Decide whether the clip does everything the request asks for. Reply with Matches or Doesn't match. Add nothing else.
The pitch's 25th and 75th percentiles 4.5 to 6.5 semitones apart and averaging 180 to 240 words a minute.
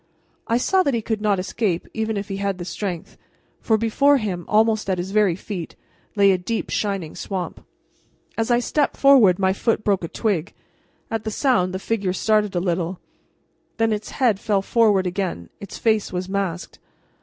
Doesn't match